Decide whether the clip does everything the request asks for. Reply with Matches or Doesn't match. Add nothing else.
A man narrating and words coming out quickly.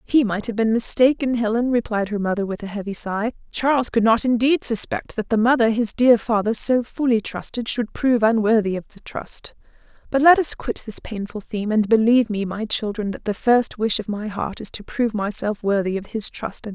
Doesn't match